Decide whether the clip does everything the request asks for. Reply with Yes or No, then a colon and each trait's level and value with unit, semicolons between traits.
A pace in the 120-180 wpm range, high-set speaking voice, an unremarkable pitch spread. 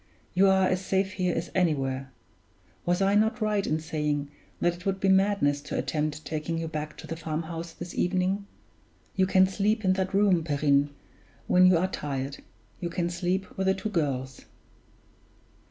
No: average, 175 wpm; medium, 175 Hz; average, 3.8 semitones